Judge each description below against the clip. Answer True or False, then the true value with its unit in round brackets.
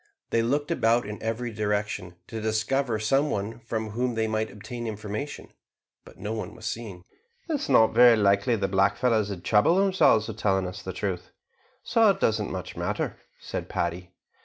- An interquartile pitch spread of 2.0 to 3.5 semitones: True (2.9 semitones)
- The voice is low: True (110 Hz)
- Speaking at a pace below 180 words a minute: False (185 wpm)